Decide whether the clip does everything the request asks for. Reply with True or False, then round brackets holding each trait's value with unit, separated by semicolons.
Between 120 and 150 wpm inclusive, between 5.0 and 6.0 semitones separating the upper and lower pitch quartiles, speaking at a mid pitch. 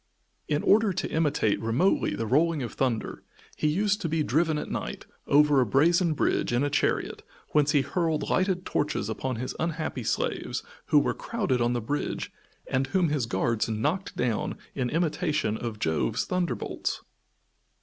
False (170 wpm; 5.4 semitones; 150 Hz)